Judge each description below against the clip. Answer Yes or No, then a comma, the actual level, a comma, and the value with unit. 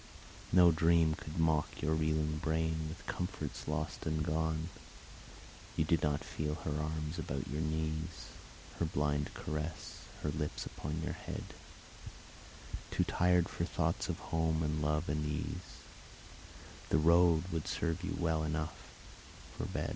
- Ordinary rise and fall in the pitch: No, narrow, 1.2 semitones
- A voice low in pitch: Yes, very low, 80 Hz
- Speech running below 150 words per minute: Yes, average, 140 wpm